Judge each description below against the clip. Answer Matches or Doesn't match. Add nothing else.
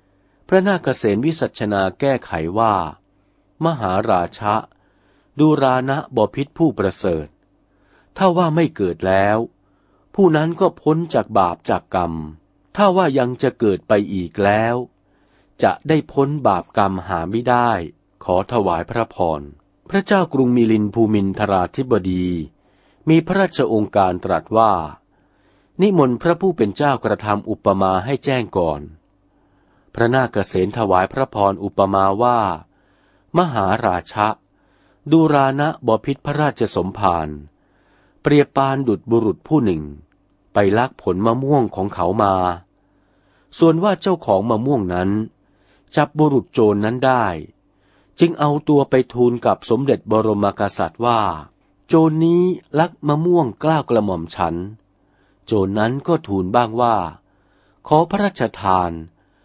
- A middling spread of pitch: Doesn't match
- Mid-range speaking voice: Doesn't match